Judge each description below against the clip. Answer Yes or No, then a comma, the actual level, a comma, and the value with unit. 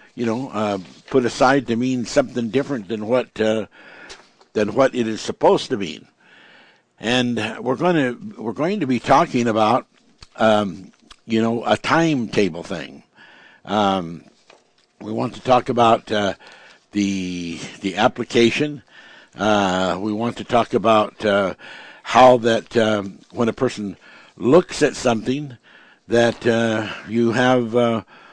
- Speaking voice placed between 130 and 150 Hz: No, low, 115 Hz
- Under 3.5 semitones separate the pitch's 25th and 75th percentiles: Yes, average, 2.9 semitones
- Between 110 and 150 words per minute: Yes, average, 140 wpm